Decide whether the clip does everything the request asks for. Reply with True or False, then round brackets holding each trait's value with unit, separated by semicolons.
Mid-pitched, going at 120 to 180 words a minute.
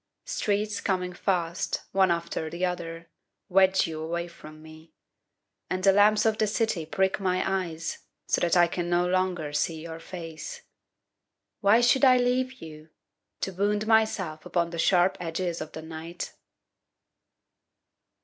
True (180 Hz; 150 wpm)